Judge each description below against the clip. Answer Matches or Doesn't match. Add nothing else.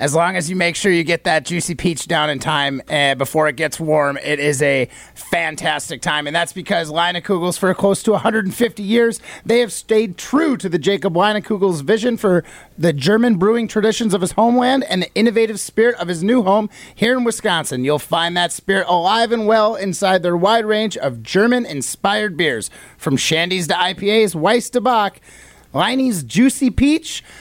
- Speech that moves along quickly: Doesn't match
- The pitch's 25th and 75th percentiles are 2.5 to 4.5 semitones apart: Doesn't match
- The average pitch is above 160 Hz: Matches